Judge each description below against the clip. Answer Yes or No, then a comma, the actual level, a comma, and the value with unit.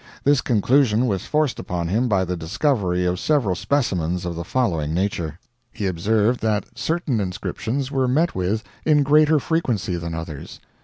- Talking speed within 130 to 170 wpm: Yes, average, 160 wpm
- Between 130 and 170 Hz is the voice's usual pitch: No, low, 105 Hz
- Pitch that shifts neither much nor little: No, wide, 7.1 semitones